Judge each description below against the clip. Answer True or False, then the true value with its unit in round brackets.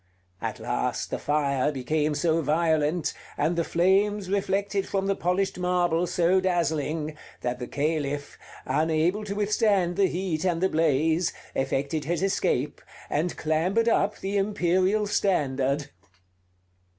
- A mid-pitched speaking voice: True (170 Hz)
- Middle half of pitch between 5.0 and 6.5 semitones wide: False (4.2 semitones)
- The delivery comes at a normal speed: False (130 wpm)